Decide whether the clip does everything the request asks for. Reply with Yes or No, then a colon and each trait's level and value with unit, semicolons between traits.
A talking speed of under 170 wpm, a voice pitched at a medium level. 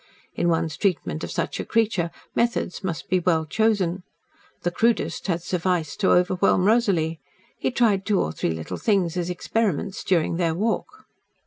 Yes: average, 160 wpm; medium, 180 Hz